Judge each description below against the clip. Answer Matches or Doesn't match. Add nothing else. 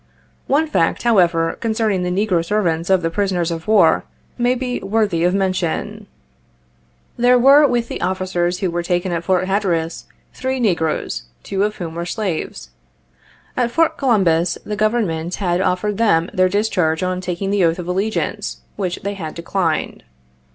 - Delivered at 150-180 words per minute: Matches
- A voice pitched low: Doesn't match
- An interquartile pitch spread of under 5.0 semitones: Matches